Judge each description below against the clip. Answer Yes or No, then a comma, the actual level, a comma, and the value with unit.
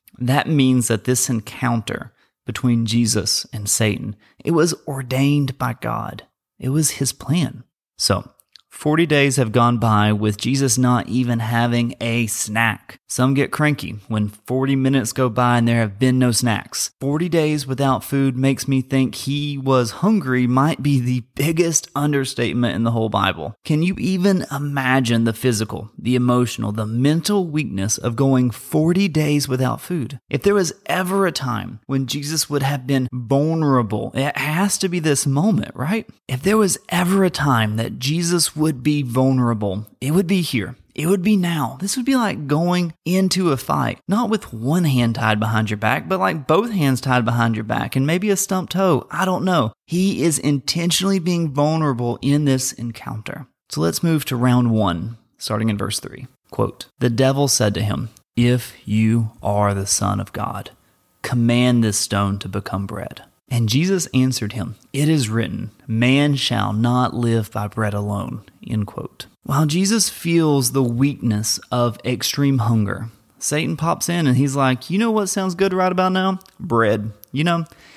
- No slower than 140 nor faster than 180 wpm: Yes, average, 175 wpm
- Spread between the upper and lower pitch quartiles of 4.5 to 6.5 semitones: Yes, average, 5.1 semitones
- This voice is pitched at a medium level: No, low, 130 Hz